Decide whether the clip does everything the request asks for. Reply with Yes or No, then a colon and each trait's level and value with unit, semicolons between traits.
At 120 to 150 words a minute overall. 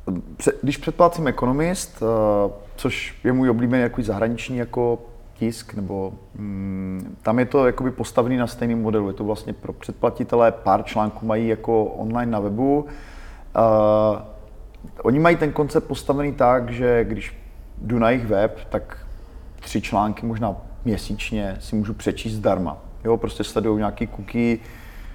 Yes: average, 140 wpm